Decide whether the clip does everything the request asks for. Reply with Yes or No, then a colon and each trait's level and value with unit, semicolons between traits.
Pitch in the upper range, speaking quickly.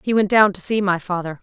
Yes: high, 195 Hz; fast, 295 wpm